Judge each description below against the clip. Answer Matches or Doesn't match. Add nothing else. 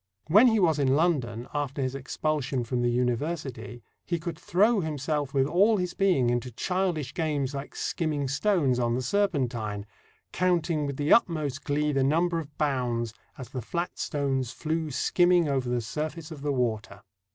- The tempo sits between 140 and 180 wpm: Matches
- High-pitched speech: Doesn't match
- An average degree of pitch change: Matches